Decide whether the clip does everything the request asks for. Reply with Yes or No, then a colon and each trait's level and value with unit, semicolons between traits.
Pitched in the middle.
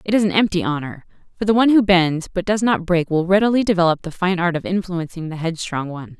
Yes: medium, 180 Hz